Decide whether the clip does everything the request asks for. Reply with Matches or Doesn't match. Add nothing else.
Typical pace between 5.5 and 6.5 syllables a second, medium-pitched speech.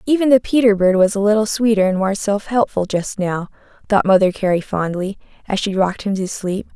Doesn't match